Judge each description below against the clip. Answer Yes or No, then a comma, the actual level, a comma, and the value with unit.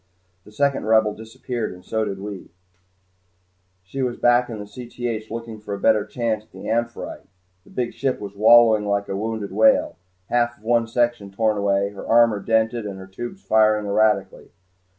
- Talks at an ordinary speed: Yes, average, 175 wpm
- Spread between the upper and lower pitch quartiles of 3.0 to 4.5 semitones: No, narrow, 2.5 semitones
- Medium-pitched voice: No, low, 110 Hz